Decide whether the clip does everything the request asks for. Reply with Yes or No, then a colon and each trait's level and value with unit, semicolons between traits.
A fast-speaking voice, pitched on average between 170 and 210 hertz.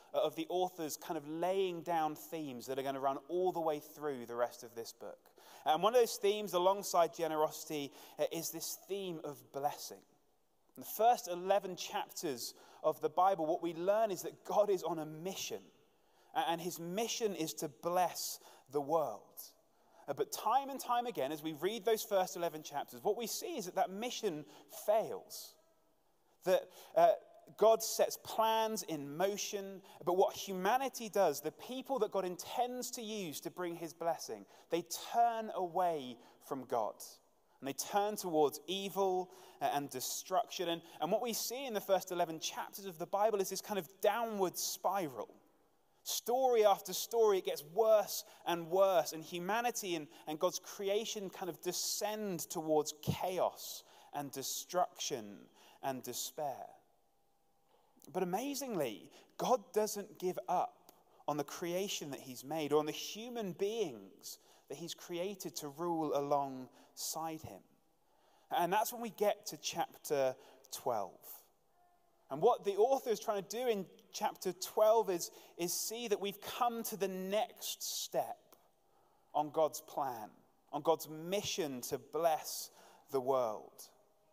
No: average, 155 wpm; medium, 185 Hz